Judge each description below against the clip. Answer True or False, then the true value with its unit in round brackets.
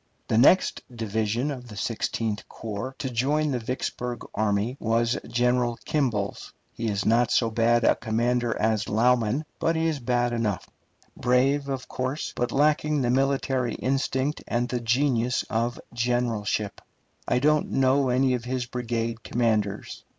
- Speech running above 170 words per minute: False (150 wpm)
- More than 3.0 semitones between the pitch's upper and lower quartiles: False (2.5 semitones)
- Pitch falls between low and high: False (120 Hz)